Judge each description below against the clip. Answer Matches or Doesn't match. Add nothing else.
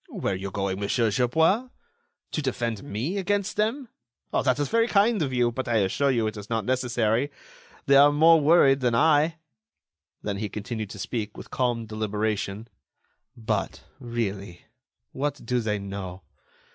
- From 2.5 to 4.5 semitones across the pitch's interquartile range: Doesn't match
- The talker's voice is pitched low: Matches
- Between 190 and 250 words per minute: Doesn't match